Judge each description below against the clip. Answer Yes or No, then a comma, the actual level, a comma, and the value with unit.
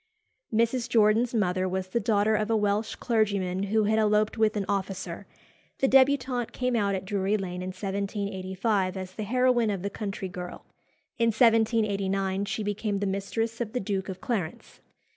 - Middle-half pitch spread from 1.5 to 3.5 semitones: Yes, average, 2.8 semitones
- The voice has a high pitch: Yes, high, 205 Hz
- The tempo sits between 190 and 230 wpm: No, average, 170 wpm